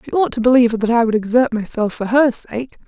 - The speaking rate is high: Yes, fast, 250 wpm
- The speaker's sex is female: Yes, female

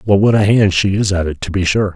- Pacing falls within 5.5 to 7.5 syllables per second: Yes, 6.1 syllables/s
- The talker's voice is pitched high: No, very low, 95 Hz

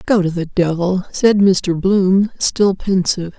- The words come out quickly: No, average, 160 wpm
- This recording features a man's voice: No, female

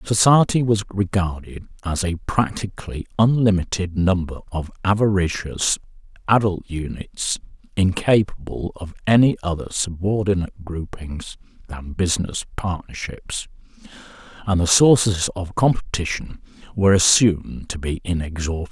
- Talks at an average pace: No, slow, 100 wpm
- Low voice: Yes, very low, 95 Hz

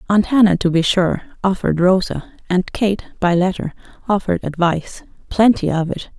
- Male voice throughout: No, female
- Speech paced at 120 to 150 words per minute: Yes, average, 145 wpm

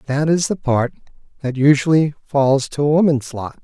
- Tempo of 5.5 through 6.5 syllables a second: No, 4.7 syllables/s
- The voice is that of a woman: No, male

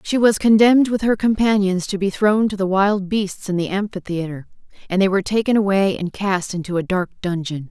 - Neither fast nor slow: No, fast, 210 wpm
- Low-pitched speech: No, high, 195 Hz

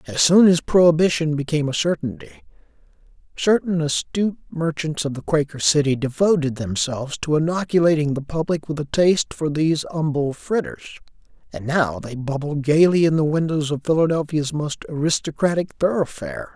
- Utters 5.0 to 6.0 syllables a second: Yes, 5.5 syllables/s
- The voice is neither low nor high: Yes, medium, 155 Hz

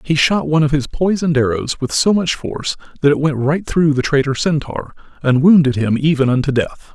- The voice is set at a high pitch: No, medium, 145 Hz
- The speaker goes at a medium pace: No, fast, 215 wpm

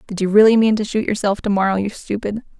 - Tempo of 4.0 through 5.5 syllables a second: No, 6.5 syllables/s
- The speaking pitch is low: No, high, 210 Hz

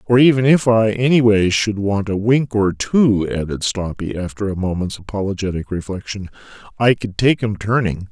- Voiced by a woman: No, male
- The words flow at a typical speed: Yes, average, 180 wpm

